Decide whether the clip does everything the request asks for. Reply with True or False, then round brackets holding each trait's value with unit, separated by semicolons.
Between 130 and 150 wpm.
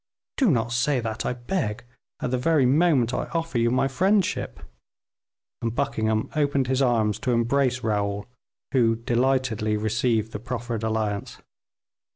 True (145 wpm)